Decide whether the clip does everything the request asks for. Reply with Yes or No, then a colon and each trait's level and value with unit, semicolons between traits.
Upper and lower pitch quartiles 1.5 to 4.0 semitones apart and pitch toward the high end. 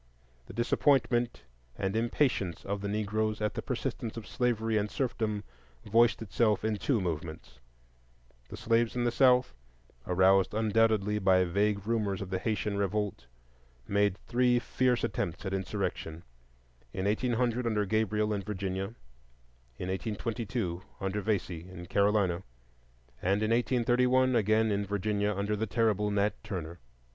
No: average, 2.9 semitones; low, 105 Hz